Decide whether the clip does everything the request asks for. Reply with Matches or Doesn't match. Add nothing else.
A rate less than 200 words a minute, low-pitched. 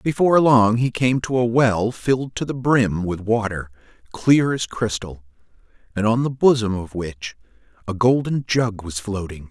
Matches